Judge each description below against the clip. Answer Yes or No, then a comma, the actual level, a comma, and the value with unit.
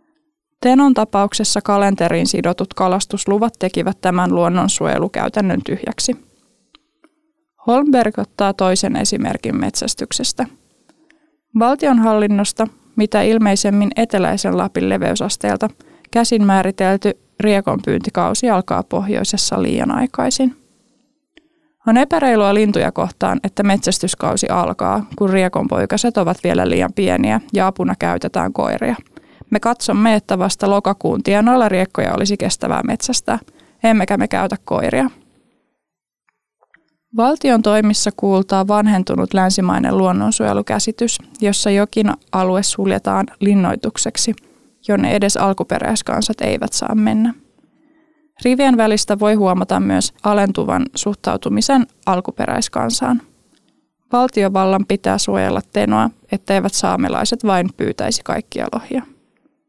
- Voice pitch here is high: Yes, high, 215 Hz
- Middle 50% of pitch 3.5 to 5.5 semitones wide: Yes, average, 4.4 semitones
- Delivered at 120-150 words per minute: No, slow, 95 wpm